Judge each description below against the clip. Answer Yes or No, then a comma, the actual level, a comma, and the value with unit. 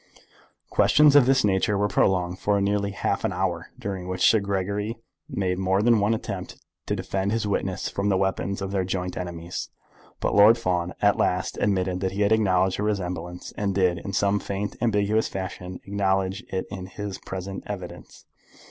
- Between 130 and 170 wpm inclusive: No, average, 180 wpm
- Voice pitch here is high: No, very low, 95 Hz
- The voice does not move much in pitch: Yes, narrow, 1.8 semitones